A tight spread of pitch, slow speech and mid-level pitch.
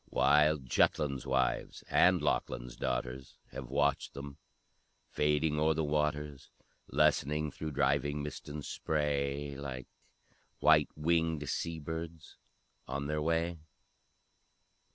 No: narrow, 1.8 semitones; slow, 110 wpm; very low, 75 Hz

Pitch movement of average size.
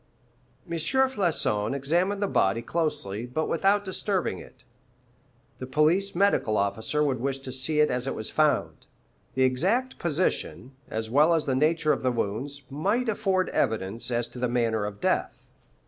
No: wide, 6.6 semitones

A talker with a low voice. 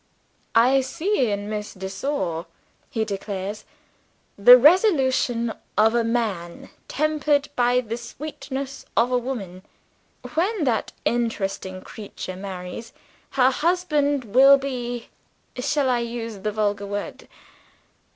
No: high, 235 Hz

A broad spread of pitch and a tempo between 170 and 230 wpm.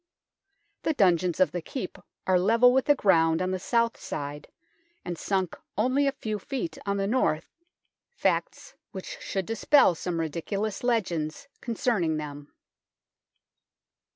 No: wide, 5.8 semitones; average, 155 wpm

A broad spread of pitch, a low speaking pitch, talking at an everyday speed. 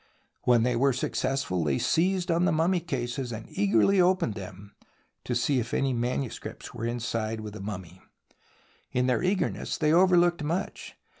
Yes: wide, 7.4 semitones; low, 125 Hz; average, 160 wpm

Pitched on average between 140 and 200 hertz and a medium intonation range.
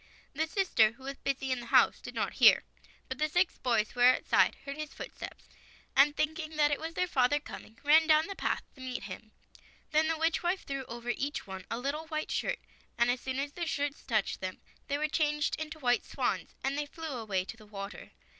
No: very high, 280 Hz; average, 4.1 semitones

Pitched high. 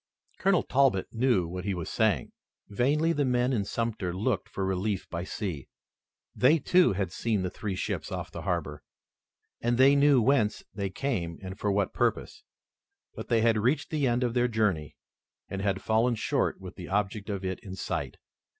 No: low, 105 Hz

